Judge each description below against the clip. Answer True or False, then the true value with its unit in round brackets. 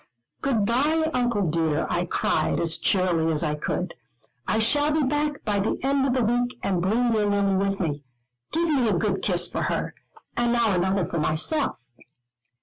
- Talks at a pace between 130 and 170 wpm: False (185 wpm)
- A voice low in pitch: False (210 Hz)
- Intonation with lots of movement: True (6.2 semitones)